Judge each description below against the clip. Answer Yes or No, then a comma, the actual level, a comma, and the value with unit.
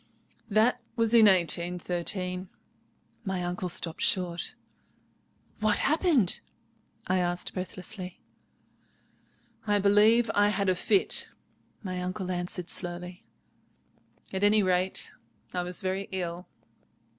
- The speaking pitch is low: No, medium, 185 Hz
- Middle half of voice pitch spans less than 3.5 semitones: Yes, narrow, 2.4 semitones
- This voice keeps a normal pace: No, slow, 105 wpm